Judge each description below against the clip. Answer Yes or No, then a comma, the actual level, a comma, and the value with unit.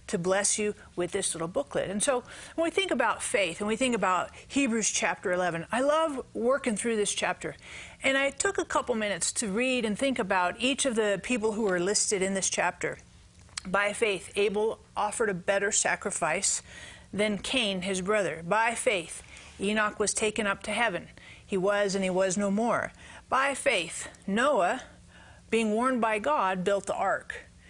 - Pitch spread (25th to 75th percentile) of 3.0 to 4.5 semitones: Yes, average, 3.9 semitones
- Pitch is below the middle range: No, high, 210 Hz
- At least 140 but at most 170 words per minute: No, average, 180 wpm